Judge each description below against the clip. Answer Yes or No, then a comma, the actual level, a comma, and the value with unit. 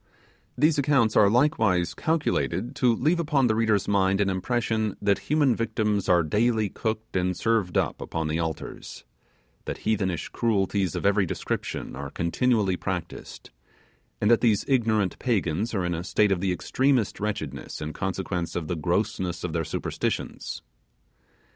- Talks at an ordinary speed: Yes, average, 155 wpm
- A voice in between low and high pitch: No, low, 105 Hz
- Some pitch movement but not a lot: Yes, average, 4.4 semitones